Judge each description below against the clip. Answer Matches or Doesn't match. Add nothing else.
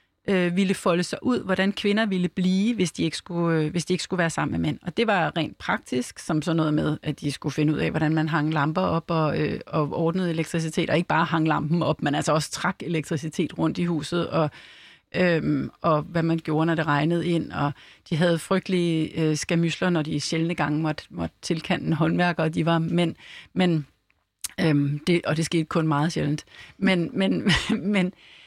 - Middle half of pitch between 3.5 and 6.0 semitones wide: Doesn't match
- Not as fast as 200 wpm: Doesn't match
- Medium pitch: Matches